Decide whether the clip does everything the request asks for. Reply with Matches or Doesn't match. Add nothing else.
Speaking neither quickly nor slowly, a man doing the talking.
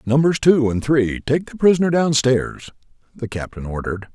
Matches